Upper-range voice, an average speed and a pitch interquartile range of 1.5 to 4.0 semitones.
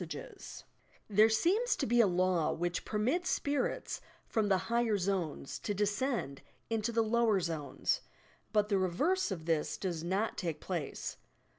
No: high, 205 Hz; average, 165 wpm; average, 4.9 semitones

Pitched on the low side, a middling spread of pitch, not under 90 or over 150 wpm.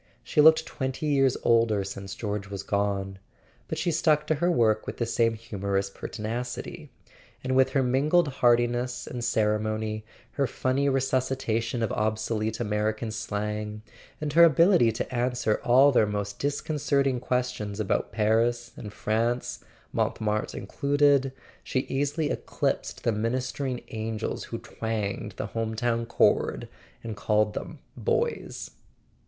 Yes: low, 115 Hz; average, 3.7 semitones; average, 140 wpm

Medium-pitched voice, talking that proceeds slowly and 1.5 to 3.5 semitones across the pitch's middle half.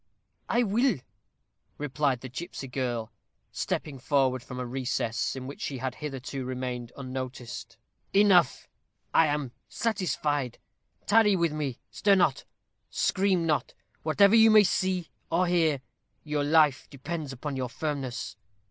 No: medium, 145 Hz; slow, 130 wpm; average, 5.1 semitones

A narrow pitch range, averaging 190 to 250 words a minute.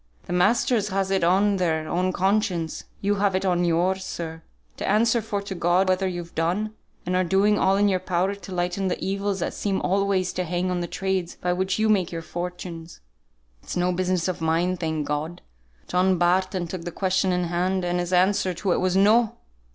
Yes: narrow, 1.9 semitones; fast, 205 wpm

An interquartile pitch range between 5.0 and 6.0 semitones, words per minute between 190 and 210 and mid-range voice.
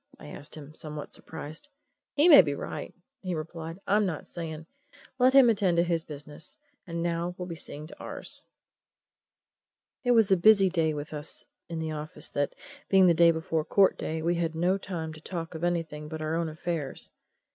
No: narrow, 2.6 semitones; average, 195 wpm; medium, 165 Hz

